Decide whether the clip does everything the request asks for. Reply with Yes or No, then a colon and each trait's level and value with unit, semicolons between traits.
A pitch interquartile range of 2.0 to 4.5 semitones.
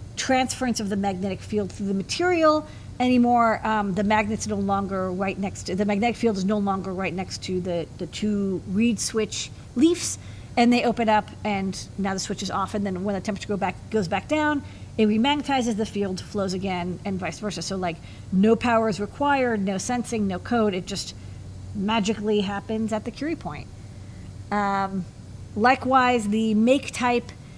Yes: average, 3.3 semitones